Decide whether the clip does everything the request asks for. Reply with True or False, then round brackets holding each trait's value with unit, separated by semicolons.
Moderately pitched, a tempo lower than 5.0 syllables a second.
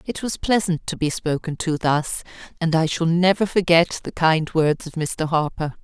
True (165 Hz; 4.6 syllables/s)